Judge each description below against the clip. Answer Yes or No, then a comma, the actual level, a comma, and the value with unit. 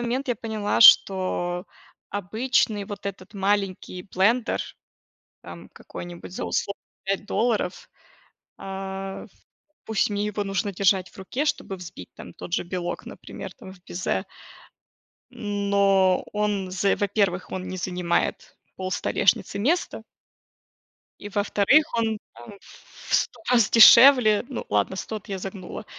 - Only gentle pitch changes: Yes, narrow, 2.3 semitones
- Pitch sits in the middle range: No, high, 200 Hz